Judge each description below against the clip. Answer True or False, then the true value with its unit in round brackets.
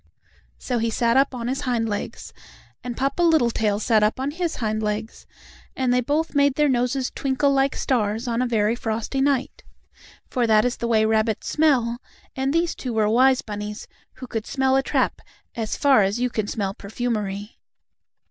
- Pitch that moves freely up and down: False (3.6 semitones)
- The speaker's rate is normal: True (180 wpm)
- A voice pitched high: True (240 Hz)